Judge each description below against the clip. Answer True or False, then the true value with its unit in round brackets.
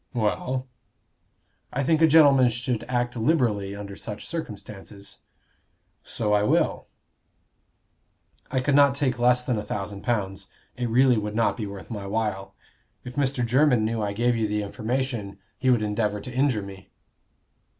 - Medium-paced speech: True (155 wpm)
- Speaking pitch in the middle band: False (115 Hz)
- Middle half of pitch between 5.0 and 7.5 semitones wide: False (3.6 semitones)